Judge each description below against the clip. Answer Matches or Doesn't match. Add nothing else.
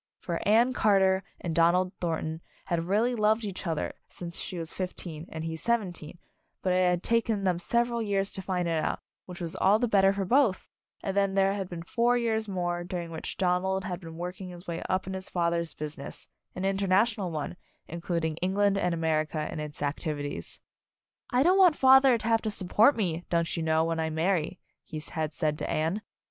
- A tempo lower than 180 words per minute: Doesn't match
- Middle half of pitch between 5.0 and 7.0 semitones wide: Doesn't match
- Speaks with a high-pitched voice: Doesn't match